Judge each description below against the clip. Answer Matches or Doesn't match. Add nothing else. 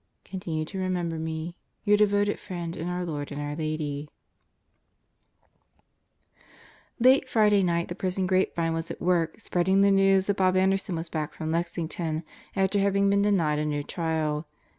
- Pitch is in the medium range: Matches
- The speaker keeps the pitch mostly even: Doesn't match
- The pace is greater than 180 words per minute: Doesn't match